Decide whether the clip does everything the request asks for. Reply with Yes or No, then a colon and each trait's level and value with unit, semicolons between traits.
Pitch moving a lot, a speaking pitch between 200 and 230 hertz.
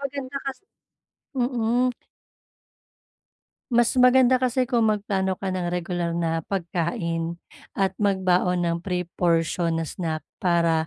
No: wide, 6.0 semitones; medium, 185 Hz